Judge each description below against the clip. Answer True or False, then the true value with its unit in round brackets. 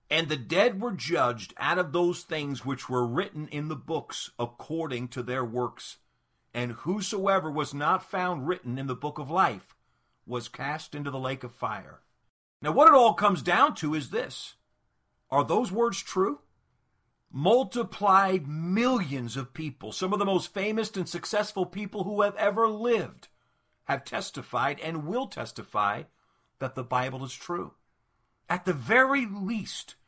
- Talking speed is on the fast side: False (160 wpm)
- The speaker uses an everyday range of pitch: False (6.9 semitones)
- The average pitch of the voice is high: False (165 Hz)